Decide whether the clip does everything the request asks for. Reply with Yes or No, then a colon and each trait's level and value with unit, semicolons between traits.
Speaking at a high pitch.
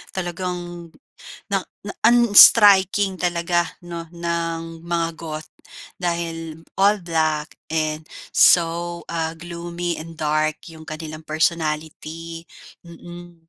No: medium, 170 Hz